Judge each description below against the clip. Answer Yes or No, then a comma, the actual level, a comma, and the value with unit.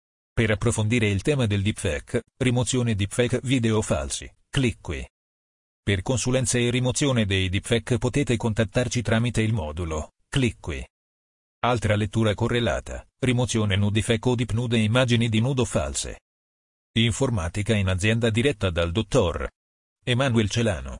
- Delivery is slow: No, average, 130 wpm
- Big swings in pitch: No, average, 3.7 semitones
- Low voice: Yes, low, 115 Hz